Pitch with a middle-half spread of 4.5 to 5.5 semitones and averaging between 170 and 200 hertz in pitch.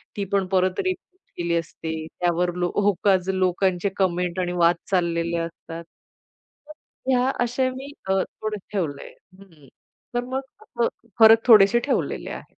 Yes: average, 5.1 semitones; high, 190 Hz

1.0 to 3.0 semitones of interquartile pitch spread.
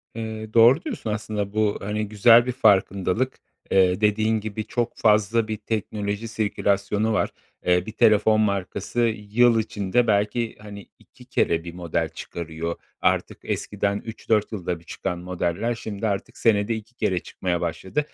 Yes: narrow, 2.5 semitones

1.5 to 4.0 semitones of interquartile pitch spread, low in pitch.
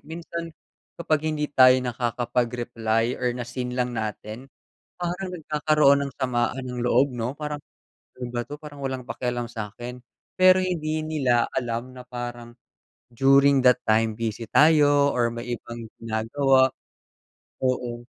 Yes: average, 3.3 semitones; low, 125 Hz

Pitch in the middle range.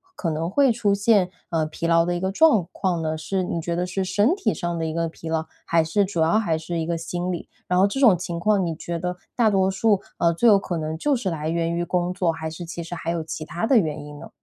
Yes: medium, 175 Hz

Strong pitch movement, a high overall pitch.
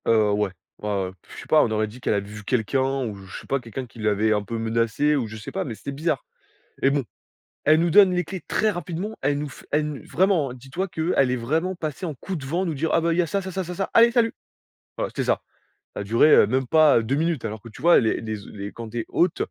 No: wide, 7.1 semitones; low, 135 Hz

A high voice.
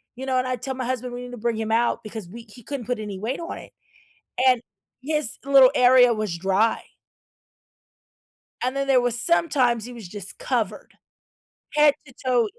Yes: high, 245 Hz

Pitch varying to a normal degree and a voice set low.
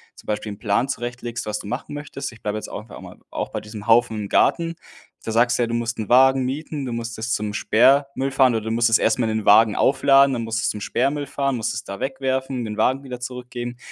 Yes: average, 3.2 semitones; low, 120 Hz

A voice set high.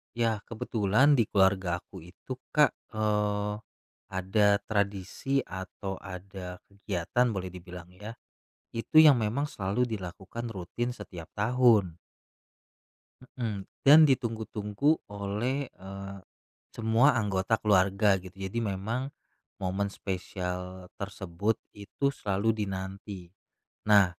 No: low, 100 Hz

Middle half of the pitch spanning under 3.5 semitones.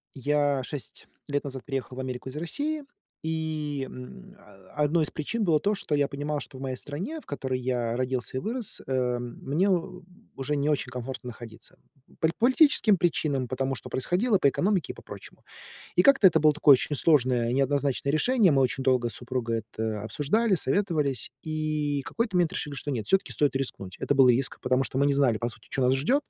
No: average, 3.9 semitones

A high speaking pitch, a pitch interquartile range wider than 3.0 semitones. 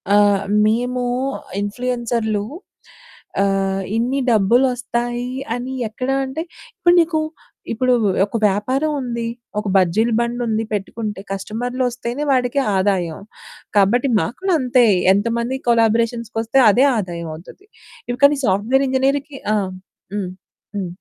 Yes: high, 235 Hz; average, 3.6 semitones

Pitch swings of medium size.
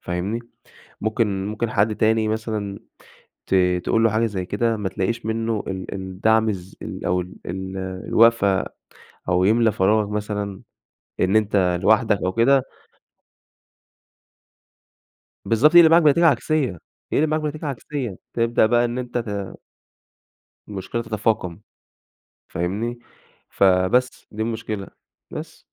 Yes: average, 3.3 semitones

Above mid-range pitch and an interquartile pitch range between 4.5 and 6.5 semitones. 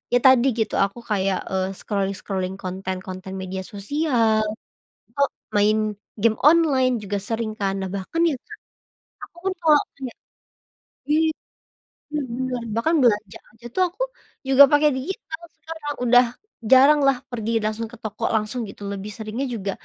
Yes: high, 230 Hz; wide, 5.5 semitones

